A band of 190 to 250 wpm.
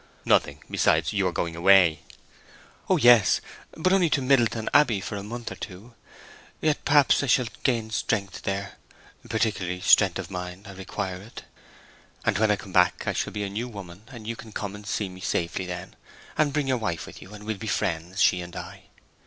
Yes: average, 195 wpm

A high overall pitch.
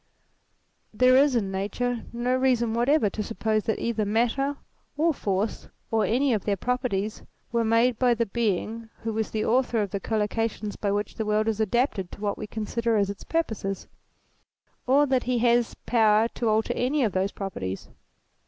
Yes: high, 225 Hz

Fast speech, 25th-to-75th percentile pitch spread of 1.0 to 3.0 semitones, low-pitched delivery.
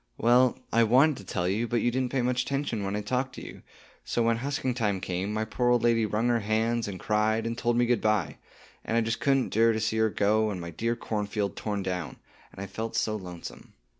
Yes: fast, 245 wpm; narrow, 2.5 semitones; low, 110 Hz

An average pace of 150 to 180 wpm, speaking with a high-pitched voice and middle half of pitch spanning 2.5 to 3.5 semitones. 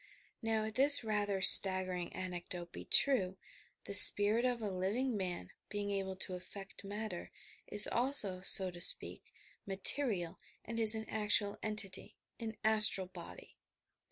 No: average, 140 wpm; high, 205 Hz; average, 2.8 semitones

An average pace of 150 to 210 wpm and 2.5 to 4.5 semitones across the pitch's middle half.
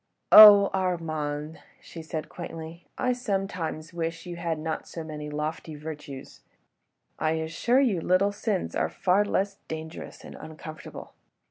No: slow, 135 wpm; average, 3.5 semitones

